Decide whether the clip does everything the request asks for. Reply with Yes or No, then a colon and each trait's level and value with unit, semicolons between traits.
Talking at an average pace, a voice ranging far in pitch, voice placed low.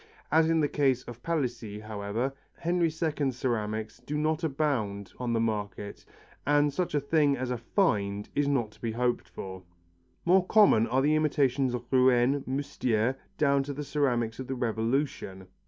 No: average, 170 wpm; average, 4.6 semitones; low, 130 Hz